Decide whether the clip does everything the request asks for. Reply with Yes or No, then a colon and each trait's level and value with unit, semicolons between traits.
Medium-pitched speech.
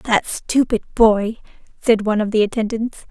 No: high, 220 Hz